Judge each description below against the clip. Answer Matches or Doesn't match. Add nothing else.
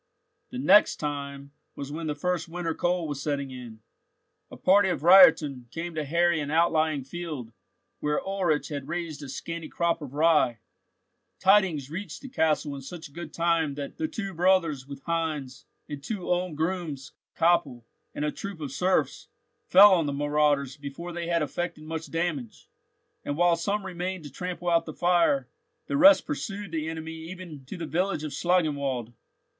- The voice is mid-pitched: Matches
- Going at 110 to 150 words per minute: Doesn't match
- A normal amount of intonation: Matches